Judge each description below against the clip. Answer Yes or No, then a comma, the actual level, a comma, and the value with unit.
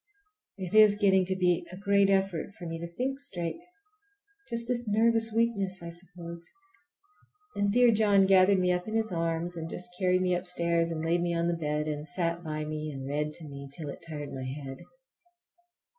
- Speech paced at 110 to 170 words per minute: No, average, 195 wpm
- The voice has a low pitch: No, medium, 175 Hz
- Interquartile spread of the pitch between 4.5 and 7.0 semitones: No, average, 3.4 semitones